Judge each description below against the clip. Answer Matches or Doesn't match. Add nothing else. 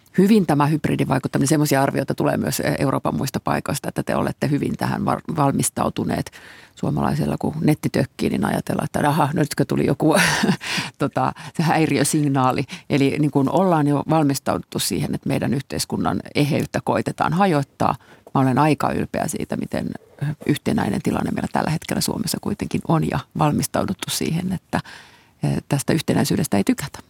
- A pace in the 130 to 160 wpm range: Matches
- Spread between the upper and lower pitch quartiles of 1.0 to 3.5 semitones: Matches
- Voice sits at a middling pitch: Matches